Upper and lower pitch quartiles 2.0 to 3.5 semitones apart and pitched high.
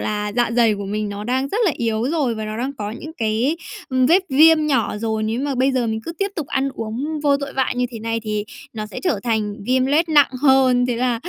No: average, 4.3 semitones; very high, 250 Hz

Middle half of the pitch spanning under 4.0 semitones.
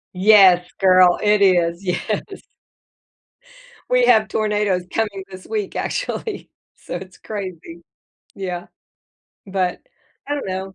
Yes: average, 2.7 semitones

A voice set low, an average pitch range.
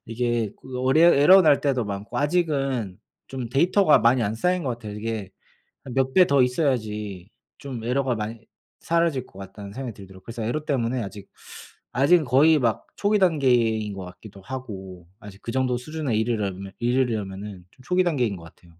Yes: low, 120 Hz; average, 4.9 semitones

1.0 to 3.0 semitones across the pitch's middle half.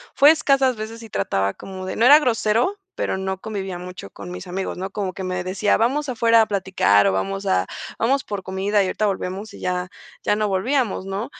No: average, 3.7 semitones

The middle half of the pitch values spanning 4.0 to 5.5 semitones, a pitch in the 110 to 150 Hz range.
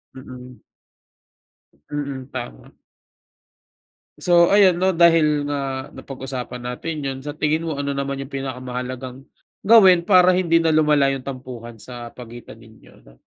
Yes: average, 4.3 semitones; medium, 140 Hz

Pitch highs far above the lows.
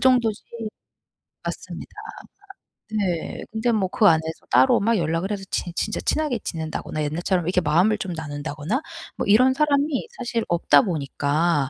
Yes: wide, 6.2 semitones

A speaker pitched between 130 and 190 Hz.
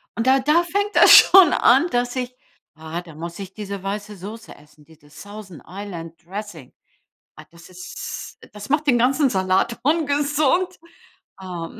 No: high, 210 Hz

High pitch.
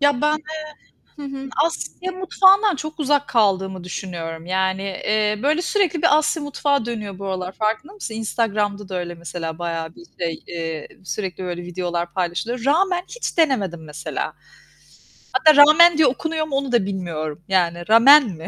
Yes: high, 215 Hz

